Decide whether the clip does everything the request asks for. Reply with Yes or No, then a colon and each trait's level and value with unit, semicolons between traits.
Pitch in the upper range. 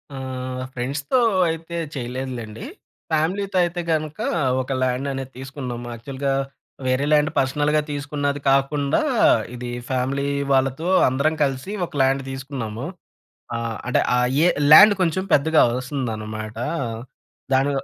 No: low, 135 Hz